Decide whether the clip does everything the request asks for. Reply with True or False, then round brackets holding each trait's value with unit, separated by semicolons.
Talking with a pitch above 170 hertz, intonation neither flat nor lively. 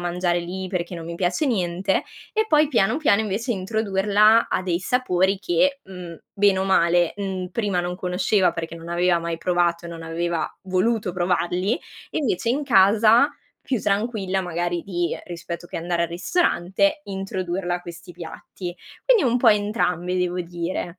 True (185 Hz; 3.2 semitones)